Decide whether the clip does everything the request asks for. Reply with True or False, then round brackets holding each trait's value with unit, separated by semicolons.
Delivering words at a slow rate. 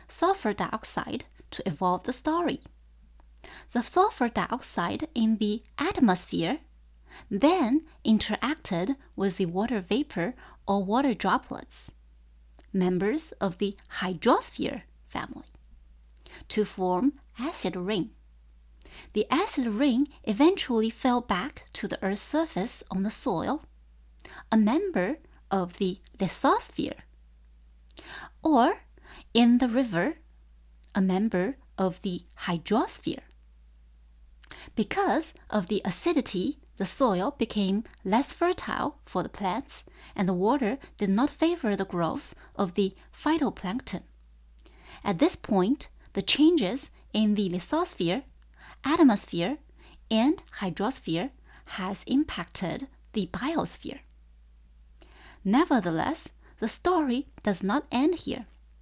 True (105 wpm)